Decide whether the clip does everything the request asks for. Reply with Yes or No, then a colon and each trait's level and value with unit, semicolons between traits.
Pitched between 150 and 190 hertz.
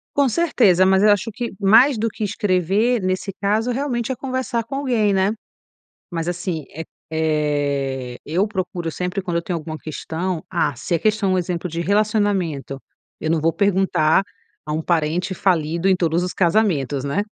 Yes: medium, 185 Hz